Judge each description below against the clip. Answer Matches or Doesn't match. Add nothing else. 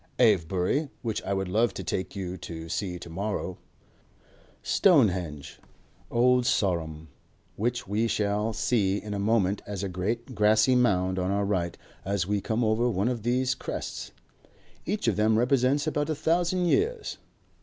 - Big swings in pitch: Doesn't match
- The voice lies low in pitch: Matches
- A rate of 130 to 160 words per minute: Matches